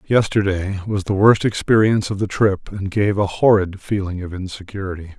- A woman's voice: No, male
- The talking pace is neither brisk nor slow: Yes, average, 175 wpm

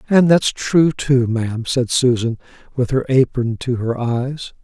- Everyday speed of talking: Yes, average, 170 wpm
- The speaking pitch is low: Yes, low, 130 Hz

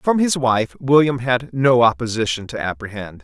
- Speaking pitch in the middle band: No, low, 120 Hz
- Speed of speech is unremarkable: Yes, average, 165 wpm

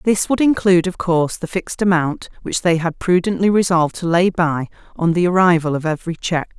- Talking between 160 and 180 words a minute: No, average, 200 wpm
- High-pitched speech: No, medium, 175 Hz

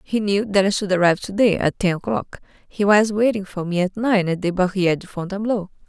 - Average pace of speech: No, fast, 235 wpm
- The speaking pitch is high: Yes, high, 195 Hz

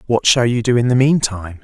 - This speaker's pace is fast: Yes, fast, 255 wpm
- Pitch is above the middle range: No, low, 115 Hz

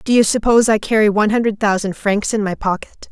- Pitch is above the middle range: Yes, high, 210 Hz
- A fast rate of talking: Yes, fast, 230 wpm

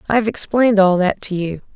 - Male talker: No, female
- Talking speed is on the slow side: No, fast, 205 wpm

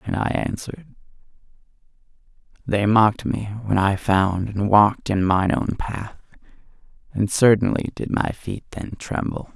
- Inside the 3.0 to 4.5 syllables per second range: Yes, 4.4 syllables/s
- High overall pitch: No, low, 105 Hz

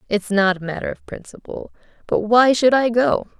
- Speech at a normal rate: Yes, average, 195 wpm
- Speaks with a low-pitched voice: No, high, 220 Hz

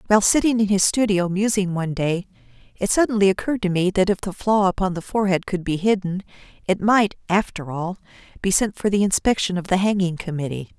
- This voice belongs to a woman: Yes, female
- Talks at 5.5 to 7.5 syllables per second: Yes, 6.0 syllables/s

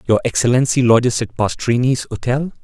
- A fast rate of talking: No, slow, 135 wpm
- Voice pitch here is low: Yes, low, 125 Hz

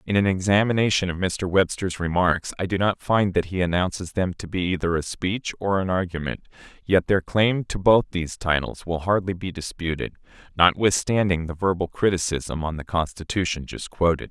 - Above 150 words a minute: Yes, average, 180 wpm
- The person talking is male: Yes, male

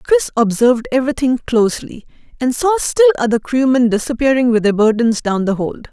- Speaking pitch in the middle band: No, high, 245 Hz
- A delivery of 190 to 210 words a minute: No, average, 160 wpm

